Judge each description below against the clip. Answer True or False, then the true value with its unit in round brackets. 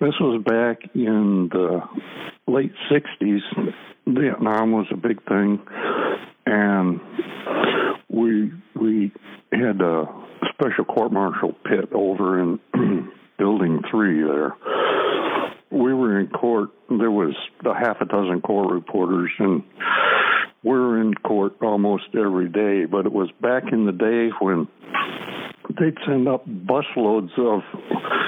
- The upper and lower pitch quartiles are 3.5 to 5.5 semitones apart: False (2.8 semitones)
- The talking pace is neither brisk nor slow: False (125 wpm)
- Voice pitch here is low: True (110 Hz)